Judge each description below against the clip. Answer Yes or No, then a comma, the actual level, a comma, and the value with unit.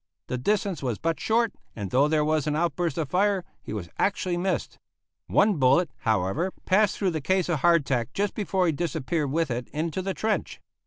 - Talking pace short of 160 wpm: No, average, 195 wpm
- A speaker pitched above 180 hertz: No, medium, 165 Hz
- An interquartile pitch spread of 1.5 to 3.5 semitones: No, wide, 5.4 semitones